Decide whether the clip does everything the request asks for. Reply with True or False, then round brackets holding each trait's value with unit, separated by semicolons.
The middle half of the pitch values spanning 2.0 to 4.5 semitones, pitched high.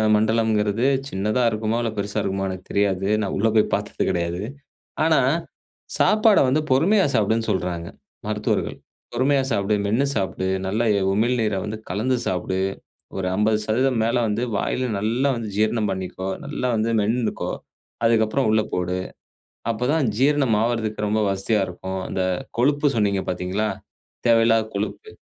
False (3.3 semitones; 110 Hz)